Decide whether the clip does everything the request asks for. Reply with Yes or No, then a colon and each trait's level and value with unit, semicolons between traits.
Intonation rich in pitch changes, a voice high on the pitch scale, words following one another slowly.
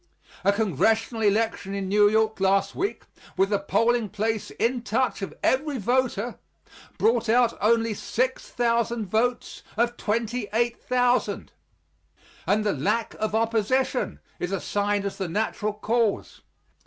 No: average, 2.7 semitones; high, 220 Hz; slow, 125 wpm